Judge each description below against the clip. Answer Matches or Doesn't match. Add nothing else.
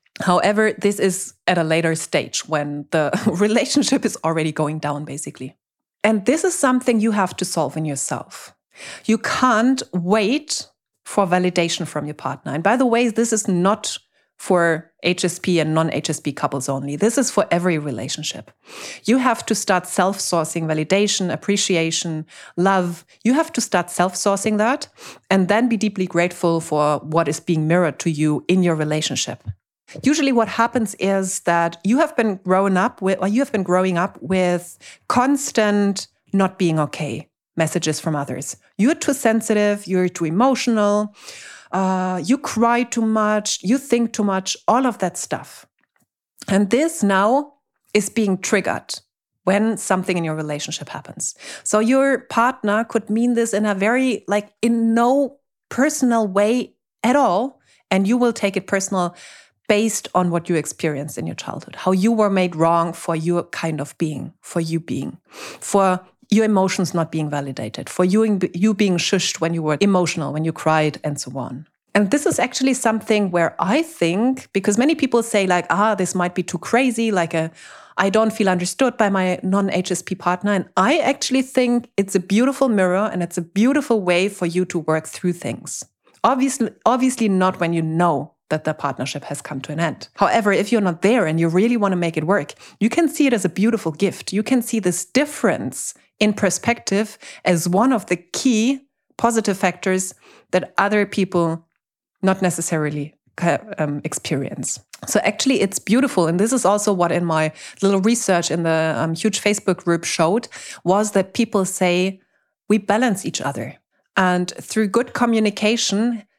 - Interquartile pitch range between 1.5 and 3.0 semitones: Doesn't match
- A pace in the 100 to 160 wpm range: Doesn't match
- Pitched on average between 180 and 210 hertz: Matches